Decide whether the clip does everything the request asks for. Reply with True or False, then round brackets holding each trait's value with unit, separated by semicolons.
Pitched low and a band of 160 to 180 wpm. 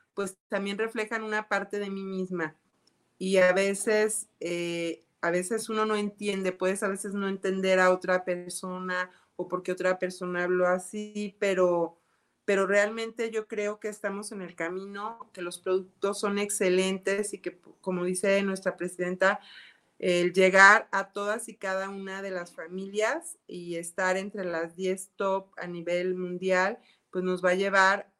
False (190 Hz; 165 wpm)